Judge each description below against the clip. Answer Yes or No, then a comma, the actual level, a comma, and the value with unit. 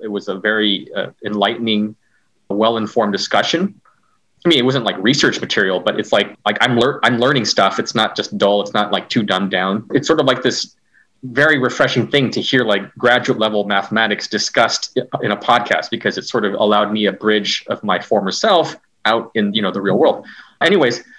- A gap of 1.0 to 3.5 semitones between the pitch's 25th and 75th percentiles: Yes, average, 2.7 semitones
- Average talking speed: No, fast, 210 wpm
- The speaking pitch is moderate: No, low, 105 Hz